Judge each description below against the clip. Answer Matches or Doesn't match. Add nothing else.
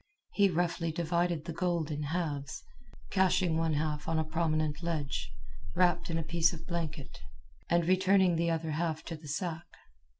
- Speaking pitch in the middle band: Matches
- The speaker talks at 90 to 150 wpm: Doesn't match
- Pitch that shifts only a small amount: Matches